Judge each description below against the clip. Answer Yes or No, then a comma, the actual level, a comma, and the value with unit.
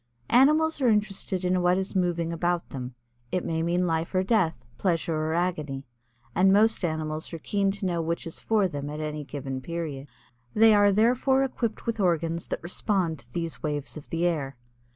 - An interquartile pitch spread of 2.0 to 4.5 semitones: Yes, average, 4.1 semitones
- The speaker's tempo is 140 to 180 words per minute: No, average, 190 wpm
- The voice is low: No, medium, 170 Hz